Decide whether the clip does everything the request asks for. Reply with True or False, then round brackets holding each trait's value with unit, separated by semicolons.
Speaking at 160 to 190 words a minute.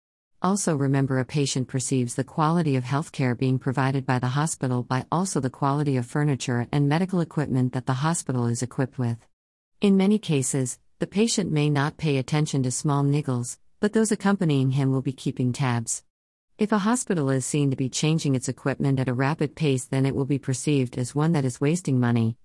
False (200 wpm)